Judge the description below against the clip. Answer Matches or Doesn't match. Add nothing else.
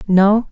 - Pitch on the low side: Doesn't match